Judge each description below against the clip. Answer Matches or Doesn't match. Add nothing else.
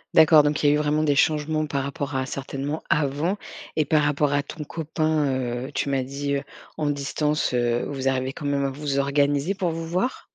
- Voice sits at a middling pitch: Matches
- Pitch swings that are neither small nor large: Doesn't match